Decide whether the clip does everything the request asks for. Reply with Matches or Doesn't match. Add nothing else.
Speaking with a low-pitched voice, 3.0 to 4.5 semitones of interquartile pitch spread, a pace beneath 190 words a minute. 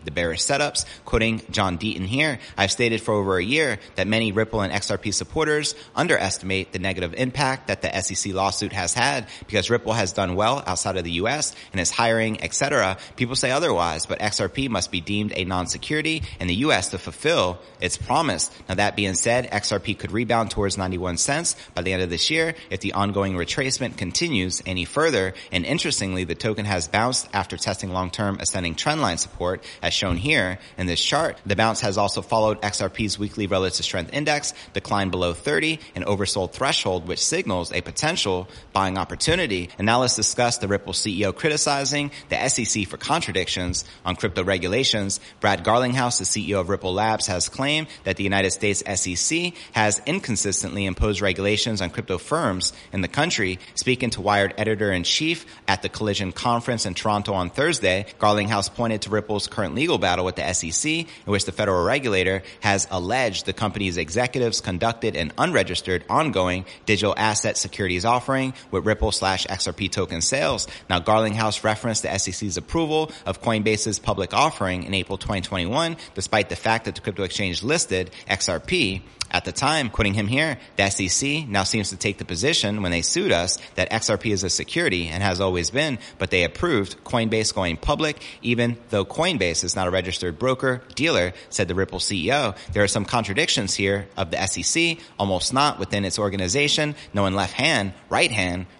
Matches